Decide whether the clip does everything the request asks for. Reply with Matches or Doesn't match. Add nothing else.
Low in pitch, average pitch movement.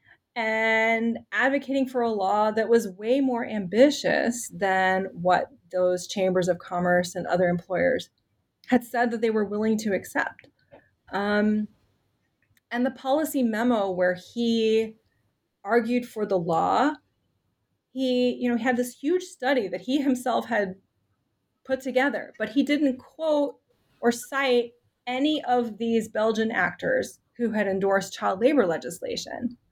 Doesn't match